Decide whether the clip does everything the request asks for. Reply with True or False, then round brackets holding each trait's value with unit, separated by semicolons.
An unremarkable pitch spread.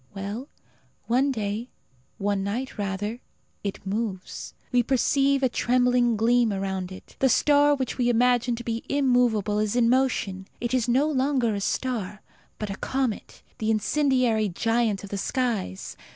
True (3.7 semitones)